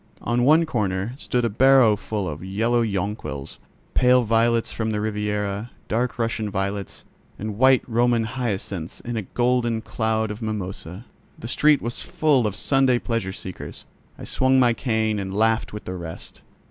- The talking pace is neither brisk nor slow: Yes, average, 160 wpm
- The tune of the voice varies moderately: Yes, average, 3.0 semitones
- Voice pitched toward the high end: No, low, 110 Hz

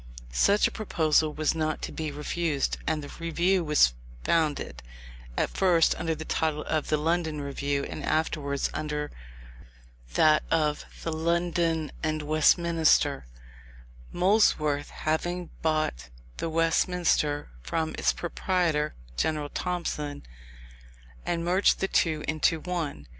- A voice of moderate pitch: Yes, medium, 155 Hz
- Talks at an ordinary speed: No, slow, 120 wpm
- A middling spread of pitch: No, narrow, 2.2 semitones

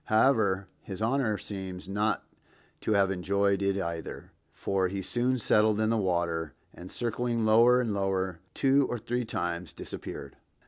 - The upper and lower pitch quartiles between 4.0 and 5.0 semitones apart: No, average, 3.3 semitones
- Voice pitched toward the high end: No, low, 100 Hz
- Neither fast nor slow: Yes, average, 150 wpm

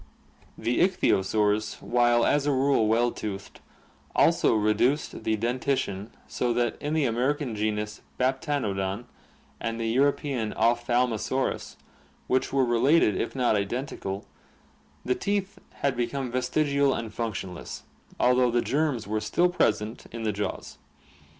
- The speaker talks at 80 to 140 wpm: Yes, slow, 135 wpm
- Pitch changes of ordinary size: Yes, average, 3.9 semitones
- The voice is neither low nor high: No, low, 120 Hz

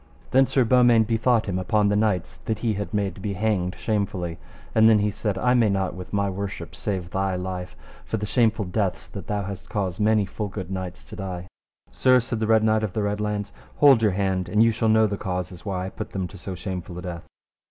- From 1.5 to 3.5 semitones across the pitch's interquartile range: Yes, average, 2.9 semitones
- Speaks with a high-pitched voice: No, low, 100 Hz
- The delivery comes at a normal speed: No, fast, 235 wpm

